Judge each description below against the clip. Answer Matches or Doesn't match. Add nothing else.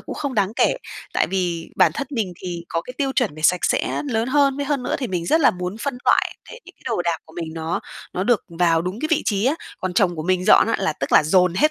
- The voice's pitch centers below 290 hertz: Matches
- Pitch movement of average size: Doesn't match